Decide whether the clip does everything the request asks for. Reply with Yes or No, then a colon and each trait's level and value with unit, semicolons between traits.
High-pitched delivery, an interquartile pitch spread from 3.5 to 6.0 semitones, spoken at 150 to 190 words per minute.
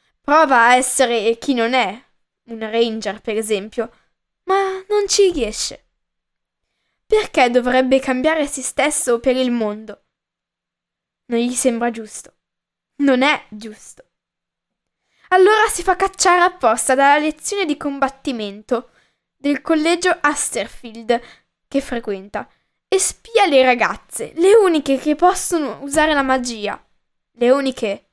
No: very high, 265 Hz; average, 5.3 semitones; average, 120 wpm